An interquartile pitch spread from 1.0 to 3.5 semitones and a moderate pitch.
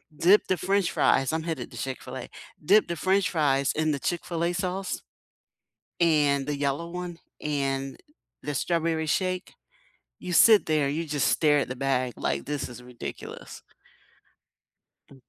No: average, 4.1 semitones; medium, 155 Hz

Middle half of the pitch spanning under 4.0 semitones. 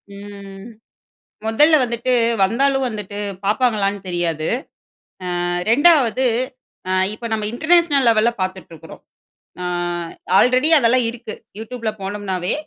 No: average, 4.4 semitones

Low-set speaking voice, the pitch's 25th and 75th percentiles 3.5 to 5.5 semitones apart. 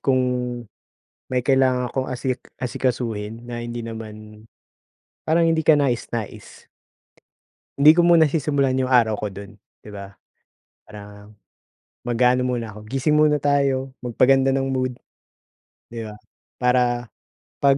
No: low, 125 Hz; average, 3.1 semitones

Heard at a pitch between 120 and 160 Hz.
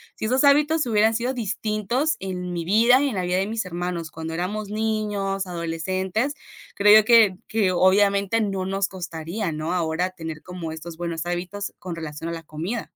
No: high, 190 Hz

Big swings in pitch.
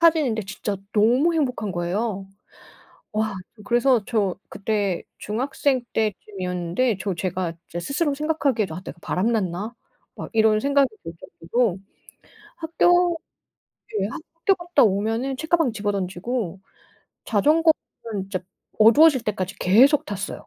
Yes: wide, 6.1 semitones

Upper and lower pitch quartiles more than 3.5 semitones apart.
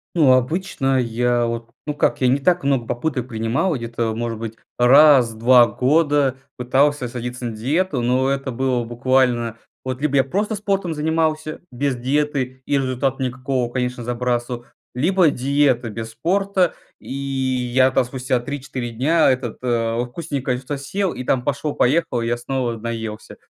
No: average, 3.0 semitones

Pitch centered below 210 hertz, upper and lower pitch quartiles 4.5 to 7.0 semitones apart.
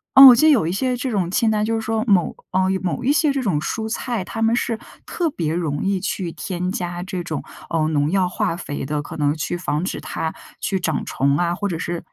Yes: medium, 185 Hz; average, 5.2 semitones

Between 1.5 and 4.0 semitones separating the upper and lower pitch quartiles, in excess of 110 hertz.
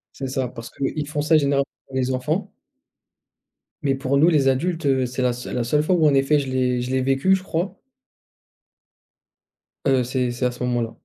Yes: average, 2.8 semitones; low, 135 Hz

